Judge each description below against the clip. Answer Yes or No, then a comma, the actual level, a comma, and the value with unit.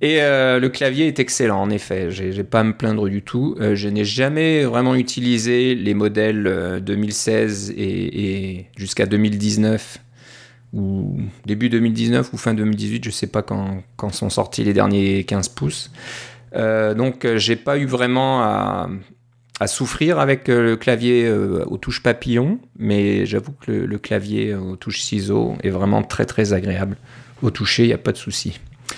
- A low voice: Yes, low, 110 Hz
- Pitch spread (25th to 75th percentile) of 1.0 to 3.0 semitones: No, average, 3.6 semitones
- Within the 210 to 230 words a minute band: No, average, 175 wpm